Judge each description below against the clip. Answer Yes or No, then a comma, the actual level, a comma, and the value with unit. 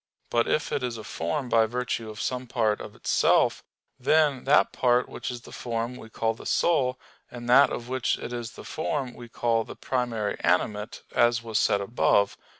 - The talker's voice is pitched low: Yes, low, 120 Hz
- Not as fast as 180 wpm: No, average, 200 wpm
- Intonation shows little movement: Yes, narrow, 2.0 semitones